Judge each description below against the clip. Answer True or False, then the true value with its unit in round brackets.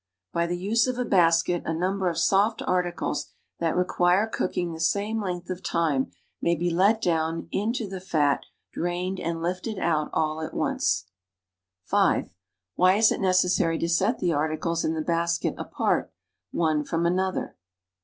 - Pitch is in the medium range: True (175 Hz)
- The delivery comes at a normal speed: False (210 wpm)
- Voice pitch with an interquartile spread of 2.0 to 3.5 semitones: True (2.4 semitones)